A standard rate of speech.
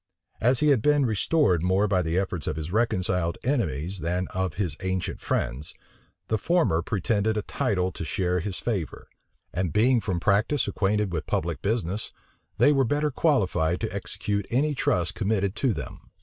Yes: average, 170 wpm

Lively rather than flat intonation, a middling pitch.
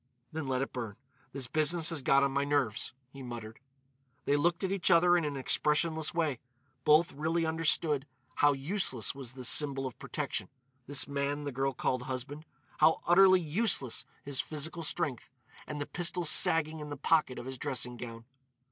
No: average, 3.5 semitones; medium, 145 Hz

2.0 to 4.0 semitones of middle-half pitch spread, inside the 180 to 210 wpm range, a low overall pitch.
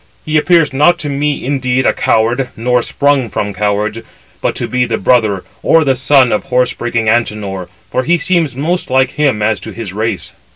No: average, 4.6 semitones; average, 195 wpm; low, 125 Hz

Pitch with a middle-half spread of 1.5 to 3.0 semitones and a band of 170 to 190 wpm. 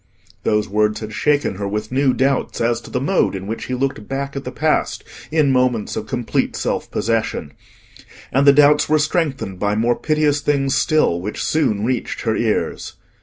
No: average, 5.1 semitones; average, 185 wpm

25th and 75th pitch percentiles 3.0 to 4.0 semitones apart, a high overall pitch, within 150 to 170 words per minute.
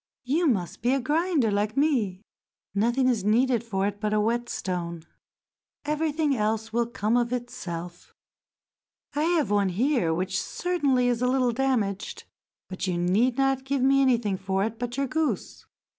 No: average, 4.9 semitones; high, 235 Hz; average, 160 wpm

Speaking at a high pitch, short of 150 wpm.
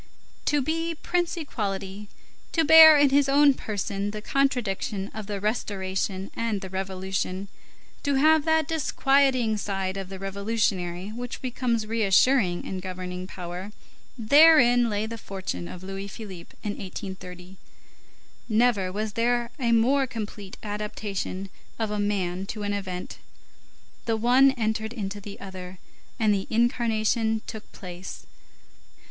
Yes: high, 210 Hz; slow, 135 wpm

